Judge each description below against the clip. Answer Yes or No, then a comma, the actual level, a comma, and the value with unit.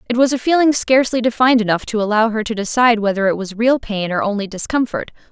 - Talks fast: Yes, fast, 225 wpm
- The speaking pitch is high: Yes, high, 225 Hz